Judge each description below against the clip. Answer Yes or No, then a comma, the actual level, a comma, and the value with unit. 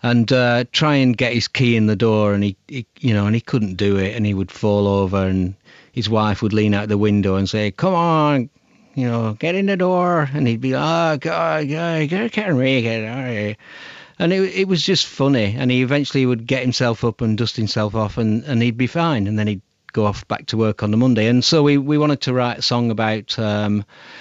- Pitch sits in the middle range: No, low, 120 Hz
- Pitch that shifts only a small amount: No, average, 5.2 semitones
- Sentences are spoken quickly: Yes, fast, 240 wpm